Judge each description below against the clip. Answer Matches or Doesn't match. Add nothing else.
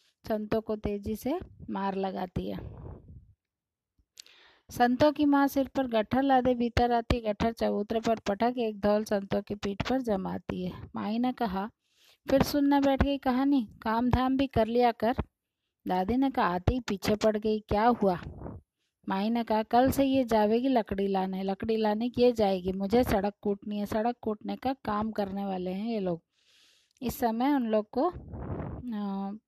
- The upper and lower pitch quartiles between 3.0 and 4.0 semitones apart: Matches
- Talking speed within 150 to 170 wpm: Matches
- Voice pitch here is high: Matches